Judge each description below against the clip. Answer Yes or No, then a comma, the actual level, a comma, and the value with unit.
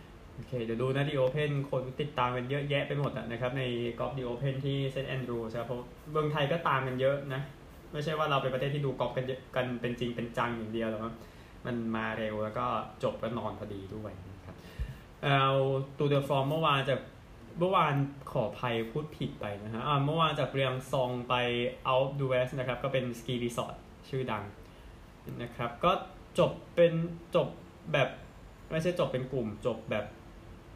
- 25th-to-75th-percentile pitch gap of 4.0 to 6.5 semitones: No, average, 3.4 semitones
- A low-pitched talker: Yes, low, 125 Hz